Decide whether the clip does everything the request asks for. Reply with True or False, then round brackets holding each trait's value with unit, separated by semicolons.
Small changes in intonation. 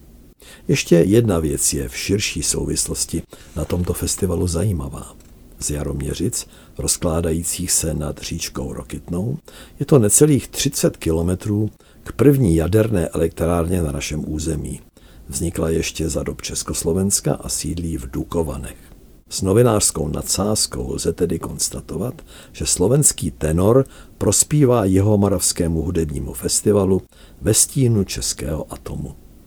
False (4.6 semitones)